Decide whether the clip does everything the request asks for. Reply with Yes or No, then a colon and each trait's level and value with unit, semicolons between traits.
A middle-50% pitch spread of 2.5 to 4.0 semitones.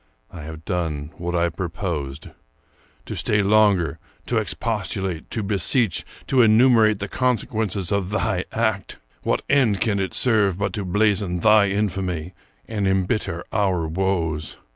Yes: average, 3.7 semitones